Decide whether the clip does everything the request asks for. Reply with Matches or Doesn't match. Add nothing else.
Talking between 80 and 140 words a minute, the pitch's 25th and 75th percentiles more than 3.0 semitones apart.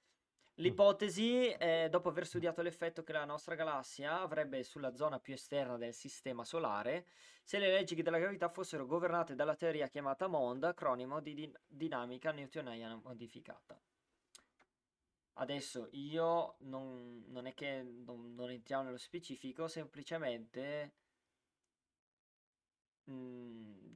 Matches